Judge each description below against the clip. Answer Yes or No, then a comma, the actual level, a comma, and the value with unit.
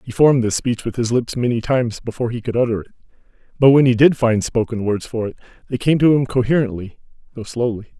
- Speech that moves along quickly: Yes, fast, 225 wpm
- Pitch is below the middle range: Yes, low, 120 Hz